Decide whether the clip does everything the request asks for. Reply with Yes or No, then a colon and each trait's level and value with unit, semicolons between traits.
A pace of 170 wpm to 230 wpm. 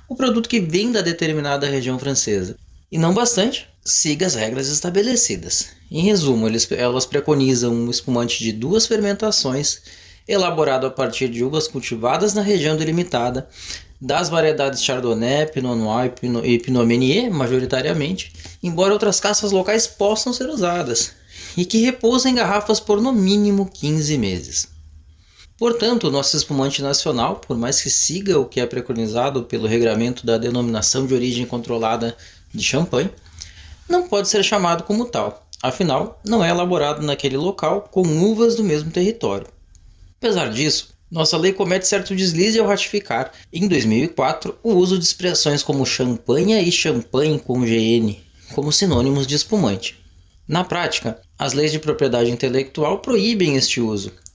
No: average, 145 wpm